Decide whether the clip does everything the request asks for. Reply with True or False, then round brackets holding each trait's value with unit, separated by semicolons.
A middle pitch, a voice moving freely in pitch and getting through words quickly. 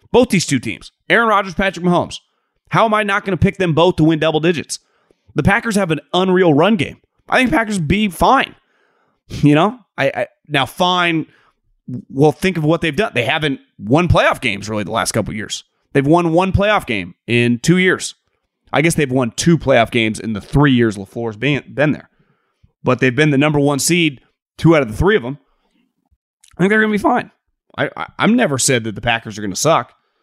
True (155 Hz; 6.2 semitones; 220 wpm)